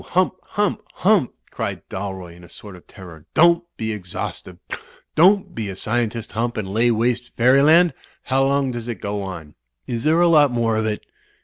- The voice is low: Yes, low, 115 Hz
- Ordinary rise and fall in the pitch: No, wide, 5.8 semitones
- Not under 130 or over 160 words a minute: No, average, 185 wpm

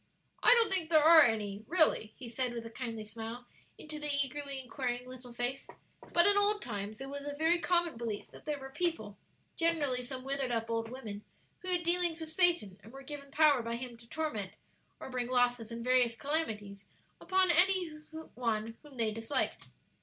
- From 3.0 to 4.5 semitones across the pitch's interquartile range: No, wide, 5.5 semitones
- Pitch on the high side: Yes, very high, 260 Hz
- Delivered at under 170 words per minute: No, average, 190 wpm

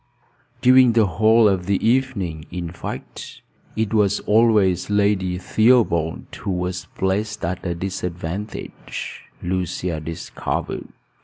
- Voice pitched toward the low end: Yes, very low, 95 Hz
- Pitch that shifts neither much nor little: Yes, average, 3.4 semitones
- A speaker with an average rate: No, slow, 110 wpm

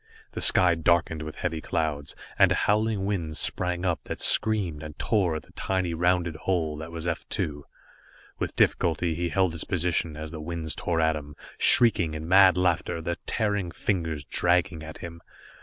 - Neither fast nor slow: Yes, average, 180 wpm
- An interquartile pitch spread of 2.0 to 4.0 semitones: Yes, narrow, 2.4 semitones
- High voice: No, very low, 85 Hz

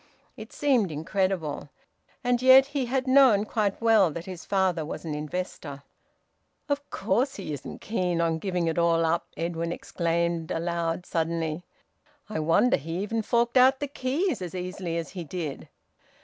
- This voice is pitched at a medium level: Yes, medium, 180 Hz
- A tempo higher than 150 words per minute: Yes, average, 160 wpm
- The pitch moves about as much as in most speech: No, wide, 6.0 semitones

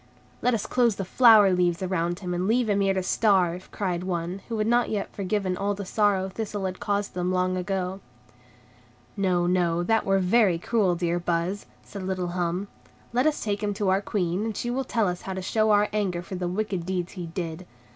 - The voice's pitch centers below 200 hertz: Yes, high, 190 Hz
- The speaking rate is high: Yes, fast, 215 wpm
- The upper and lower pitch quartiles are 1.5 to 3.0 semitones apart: Yes, narrow, 2.6 semitones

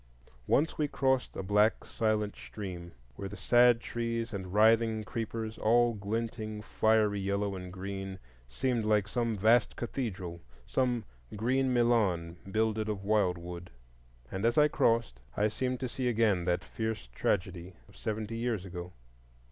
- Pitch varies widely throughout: No, average, 3.3 semitones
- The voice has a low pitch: Yes, low, 110 Hz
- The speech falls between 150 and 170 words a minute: No, average, 140 wpm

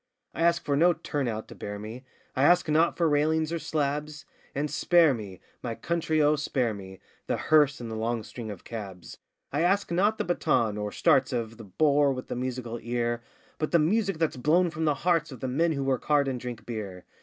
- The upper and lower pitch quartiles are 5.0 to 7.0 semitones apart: Yes, average, 5.3 semitones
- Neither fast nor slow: No, fast, 220 wpm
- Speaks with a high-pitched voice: No, medium, 140 Hz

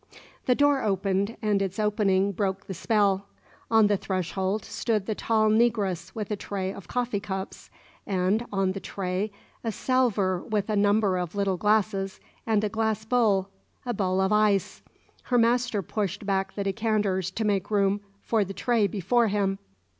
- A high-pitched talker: Yes, high, 205 Hz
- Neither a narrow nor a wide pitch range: No, narrow, 2.2 semitones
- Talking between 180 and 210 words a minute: No, average, 170 wpm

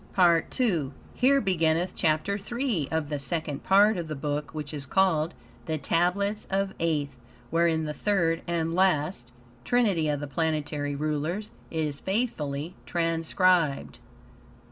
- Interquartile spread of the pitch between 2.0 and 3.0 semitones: No, average, 4.0 semitones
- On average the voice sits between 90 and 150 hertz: No, medium, 165 Hz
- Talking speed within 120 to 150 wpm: Yes, slow, 135 wpm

